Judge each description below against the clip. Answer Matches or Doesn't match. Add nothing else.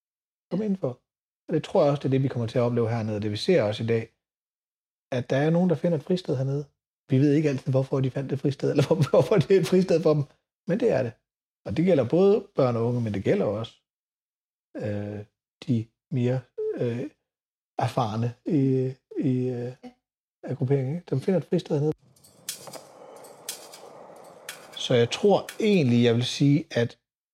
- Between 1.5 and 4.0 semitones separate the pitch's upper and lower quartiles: Doesn't match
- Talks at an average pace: Matches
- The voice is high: Doesn't match